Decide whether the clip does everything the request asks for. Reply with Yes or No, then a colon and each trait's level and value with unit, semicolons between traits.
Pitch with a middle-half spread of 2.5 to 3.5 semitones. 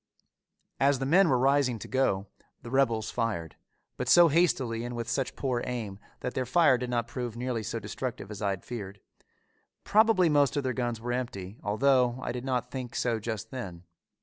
Yes: average, 2.8 semitones